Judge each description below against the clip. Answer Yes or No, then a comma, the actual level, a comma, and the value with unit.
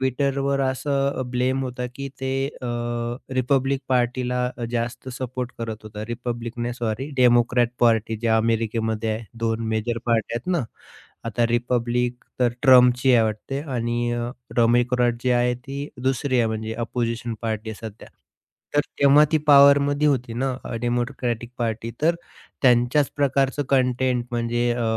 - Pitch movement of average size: No, narrow, 2.1 semitones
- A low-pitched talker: Yes, low, 120 Hz